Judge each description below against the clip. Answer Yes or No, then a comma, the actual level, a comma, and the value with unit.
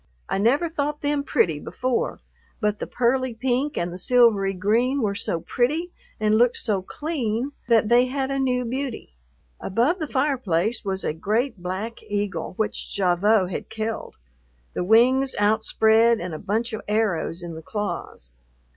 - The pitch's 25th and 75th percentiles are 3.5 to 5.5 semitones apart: Yes, average, 4.4 semitones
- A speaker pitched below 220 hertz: No, high, 225 Hz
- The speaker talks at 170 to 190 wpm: No, average, 160 wpm